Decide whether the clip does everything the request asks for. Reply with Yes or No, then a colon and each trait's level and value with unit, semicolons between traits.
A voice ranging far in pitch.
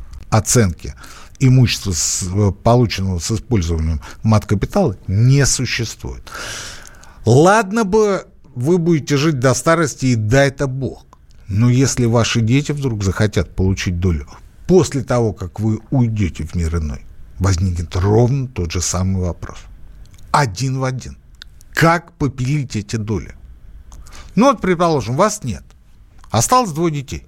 Yes: wide, 6.9 semitones